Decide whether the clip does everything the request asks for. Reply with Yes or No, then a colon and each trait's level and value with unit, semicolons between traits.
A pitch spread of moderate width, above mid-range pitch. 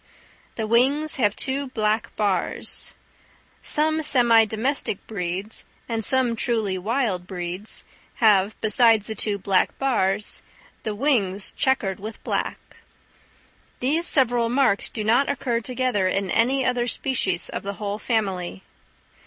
Yes: average, 4.2 semitones; high, 220 Hz